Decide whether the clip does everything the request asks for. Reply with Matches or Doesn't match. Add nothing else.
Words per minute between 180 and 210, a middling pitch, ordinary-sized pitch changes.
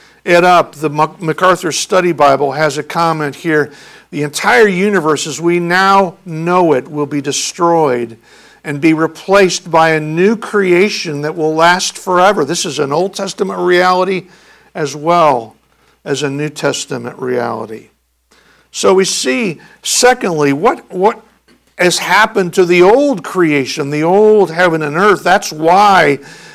Doesn't match